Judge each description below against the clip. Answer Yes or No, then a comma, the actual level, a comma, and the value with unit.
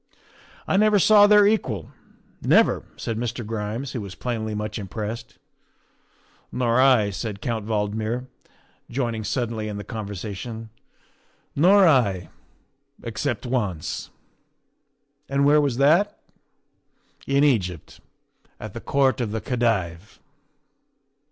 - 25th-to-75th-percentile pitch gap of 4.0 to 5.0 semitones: Yes, average, 4.4 semitones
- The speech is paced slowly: Yes, slow, 125 wpm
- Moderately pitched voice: No, low, 115 Hz